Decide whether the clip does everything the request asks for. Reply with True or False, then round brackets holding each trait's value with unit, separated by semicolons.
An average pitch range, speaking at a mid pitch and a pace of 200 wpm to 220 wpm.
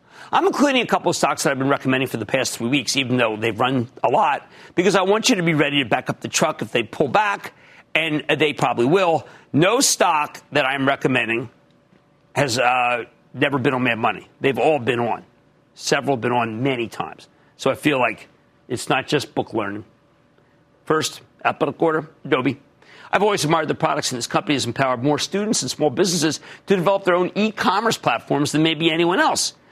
True (5.0 semitones; 145 Hz; 205 wpm)